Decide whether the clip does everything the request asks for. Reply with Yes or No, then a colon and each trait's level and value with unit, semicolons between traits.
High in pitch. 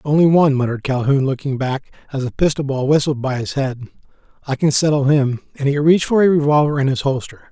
No: medium, 140 Hz